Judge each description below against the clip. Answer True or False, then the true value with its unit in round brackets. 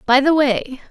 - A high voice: True (275 Hz)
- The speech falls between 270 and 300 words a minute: False (200 wpm)